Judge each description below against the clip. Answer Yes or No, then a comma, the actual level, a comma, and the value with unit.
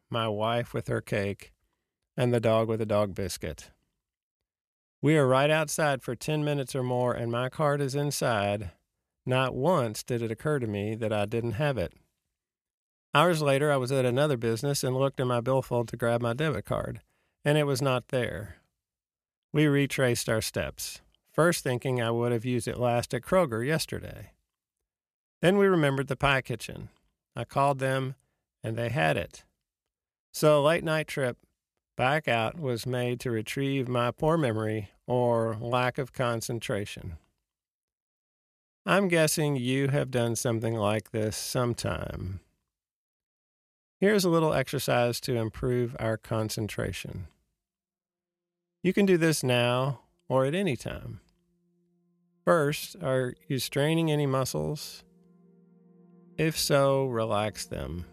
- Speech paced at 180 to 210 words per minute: No, average, 145 wpm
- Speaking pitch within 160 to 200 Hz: No, low, 125 Hz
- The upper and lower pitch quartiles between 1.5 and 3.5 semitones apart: No, average, 4.8 semitones